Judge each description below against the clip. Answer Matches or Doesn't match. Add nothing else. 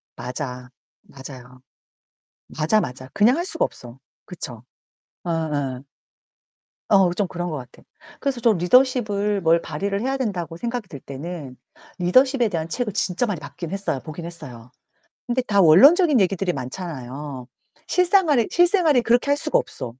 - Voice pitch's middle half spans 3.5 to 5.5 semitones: Doesn't match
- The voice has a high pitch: Doesn't match